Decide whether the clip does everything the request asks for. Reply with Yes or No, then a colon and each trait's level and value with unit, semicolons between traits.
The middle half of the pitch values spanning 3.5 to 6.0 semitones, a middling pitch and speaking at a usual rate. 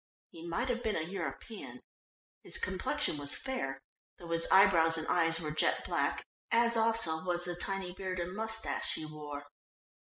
Yes: wide, 5.4 semitones; medium, 180 Hz; average, 165 wpm